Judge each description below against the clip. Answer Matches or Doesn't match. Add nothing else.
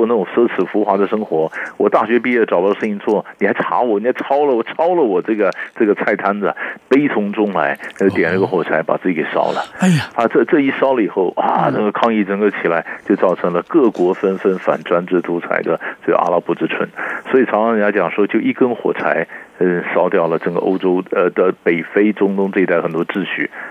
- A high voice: Doesn't match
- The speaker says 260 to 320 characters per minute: Doesn't match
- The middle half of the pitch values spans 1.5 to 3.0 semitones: Matches